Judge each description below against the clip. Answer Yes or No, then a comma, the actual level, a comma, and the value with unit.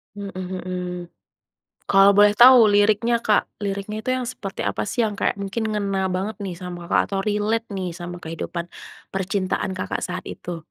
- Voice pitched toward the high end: Yes, high, 195 Hz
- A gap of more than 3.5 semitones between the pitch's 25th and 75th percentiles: No, narrow, 2.4 semitones